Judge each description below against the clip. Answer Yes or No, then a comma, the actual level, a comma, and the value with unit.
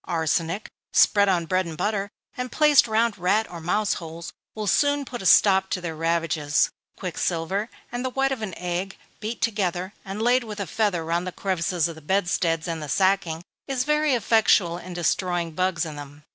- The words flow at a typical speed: Yes, average, 190 wpm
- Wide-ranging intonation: No, average, 4.4 semitones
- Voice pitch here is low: No, medium, 185 Hz